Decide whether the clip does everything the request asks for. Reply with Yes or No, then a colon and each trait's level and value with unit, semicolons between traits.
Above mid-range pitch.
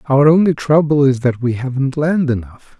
No: medium, 140 Hz